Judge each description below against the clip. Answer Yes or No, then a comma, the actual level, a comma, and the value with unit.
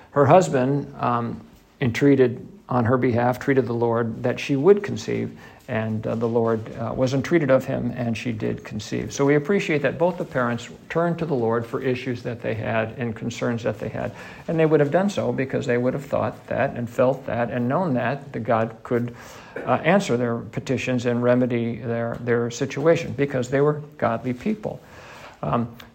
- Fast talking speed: No, average, 195 wpm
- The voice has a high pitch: No, low, 125 Hz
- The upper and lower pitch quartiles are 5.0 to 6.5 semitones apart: No, average, 3.0 semitones